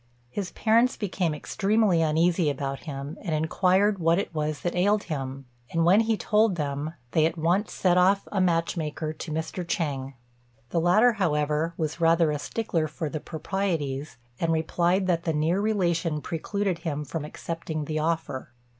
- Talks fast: No, average, 170 wpm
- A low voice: No, medium, 165 Hz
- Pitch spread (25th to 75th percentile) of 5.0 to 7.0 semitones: No, average, 3.4 semitones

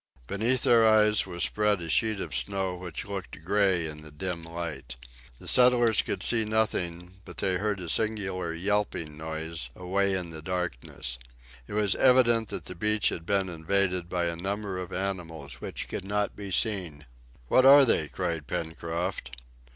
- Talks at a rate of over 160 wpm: Yes, average, 170 wpm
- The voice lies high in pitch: No, very low, 95 Hz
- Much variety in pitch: No, average, 3.8 semitones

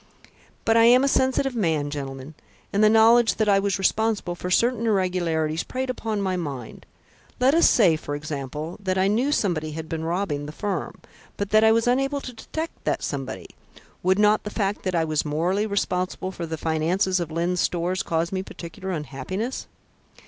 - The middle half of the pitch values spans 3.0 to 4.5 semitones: No, wide, 5.4 semitones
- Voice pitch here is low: No, medium, 185 Hz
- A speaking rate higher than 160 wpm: Yes, average, 185 wpm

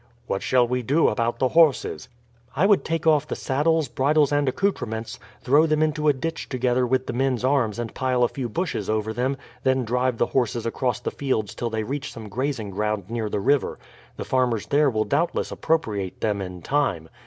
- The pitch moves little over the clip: No, average, 4.4 semitones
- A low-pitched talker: Yes, low, 130 Hz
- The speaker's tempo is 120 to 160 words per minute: No, average, 200 wpm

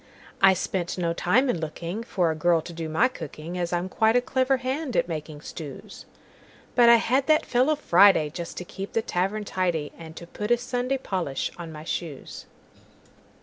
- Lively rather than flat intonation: Yes, wide, 6.5 semitones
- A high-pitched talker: No, medium, 180 Hz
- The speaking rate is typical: Yes, average, 170 wpm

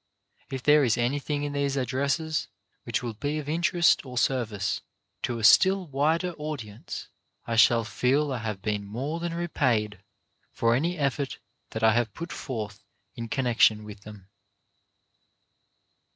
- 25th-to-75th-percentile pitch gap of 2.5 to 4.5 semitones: No, average, 5.0 semitones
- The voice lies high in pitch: No, low, 130 Hz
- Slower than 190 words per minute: Yes, average, 150 wpm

